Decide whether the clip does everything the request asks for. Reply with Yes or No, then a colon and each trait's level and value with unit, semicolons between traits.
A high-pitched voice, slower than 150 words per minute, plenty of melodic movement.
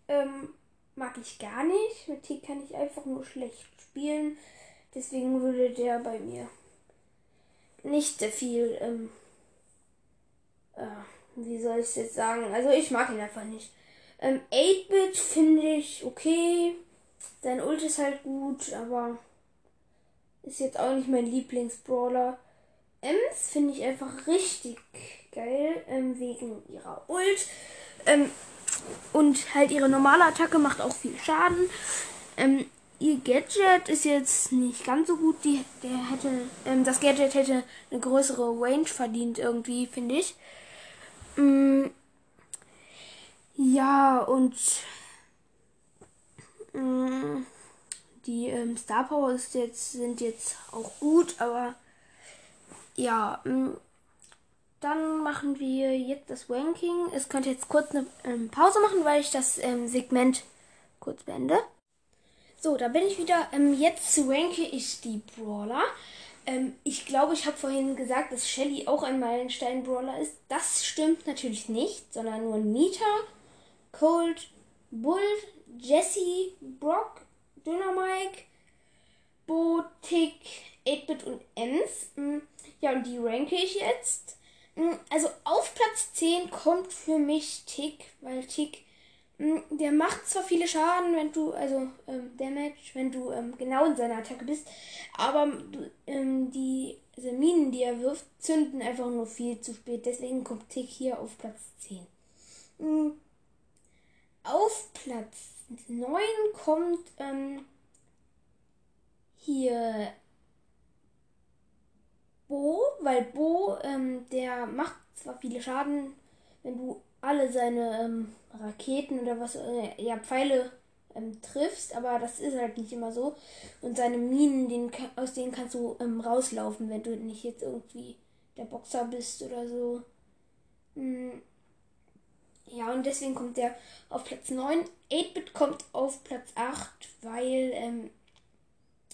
No: very high, 265 Hz; average, 130 wpm; average, 3.8 semitones